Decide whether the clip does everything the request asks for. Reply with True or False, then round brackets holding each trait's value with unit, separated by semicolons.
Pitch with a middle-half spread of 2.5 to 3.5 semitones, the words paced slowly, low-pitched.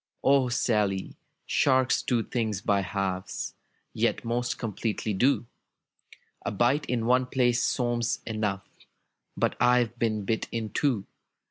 True (2.8 semitones; 125 wpm; 115 Hz)